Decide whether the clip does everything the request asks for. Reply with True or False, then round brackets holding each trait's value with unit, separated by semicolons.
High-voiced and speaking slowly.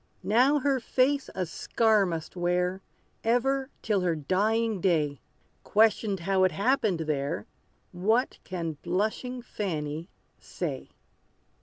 True (195 Hz; 115 wpm)